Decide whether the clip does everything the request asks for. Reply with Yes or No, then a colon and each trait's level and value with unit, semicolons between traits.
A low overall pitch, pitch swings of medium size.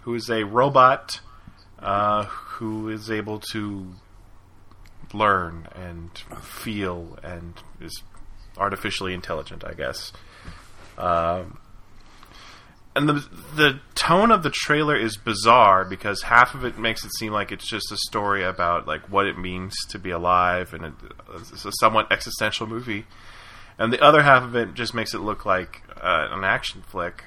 Yes: low, 105 Hz; average, 3.7 semitones